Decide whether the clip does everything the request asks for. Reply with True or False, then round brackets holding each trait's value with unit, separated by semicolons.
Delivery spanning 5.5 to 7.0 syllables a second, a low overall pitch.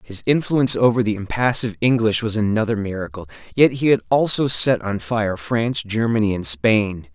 False (5.3 syllables/s; 110 Hz)